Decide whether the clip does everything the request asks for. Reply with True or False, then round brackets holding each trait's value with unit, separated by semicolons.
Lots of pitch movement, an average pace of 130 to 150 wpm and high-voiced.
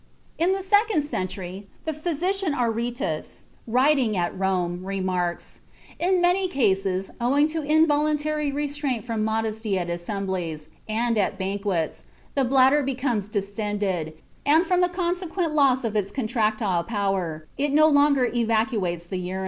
True (7.5 semitones; 135 wpm; 230 Hz)